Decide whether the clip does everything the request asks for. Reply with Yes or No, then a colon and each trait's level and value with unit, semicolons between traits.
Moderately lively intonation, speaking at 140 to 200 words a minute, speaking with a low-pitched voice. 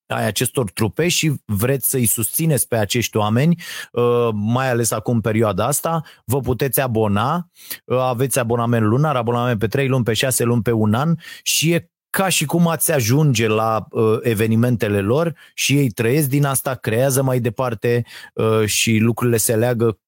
Yes: average, 3.5 semitones; average, 165 wpm; low, 120 Hz